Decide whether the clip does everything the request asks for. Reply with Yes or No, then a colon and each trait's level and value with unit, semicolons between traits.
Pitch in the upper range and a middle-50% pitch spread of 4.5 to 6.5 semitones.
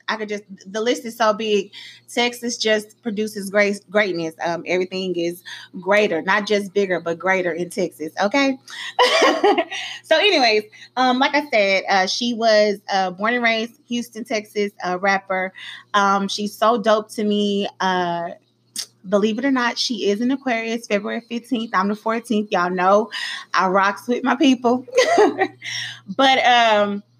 No: high, 215 Hz; average, 3.6 semitones